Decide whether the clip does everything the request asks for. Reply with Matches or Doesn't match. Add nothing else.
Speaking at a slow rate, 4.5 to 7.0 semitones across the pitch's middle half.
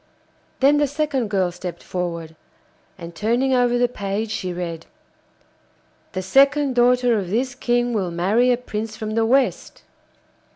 Doesn't match